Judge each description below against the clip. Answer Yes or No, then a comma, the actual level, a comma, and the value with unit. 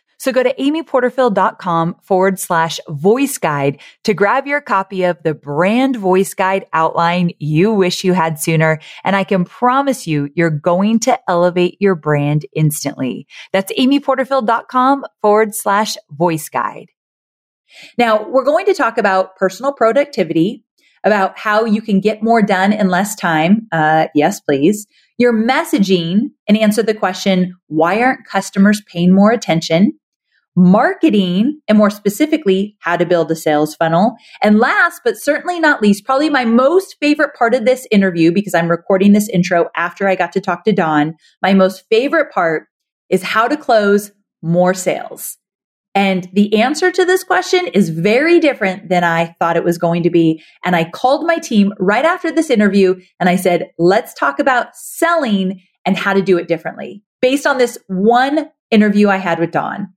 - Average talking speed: Yes, average, 170 wpm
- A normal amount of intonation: No, wide, 6.1 semitones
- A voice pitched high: Yes, high, 200 Hz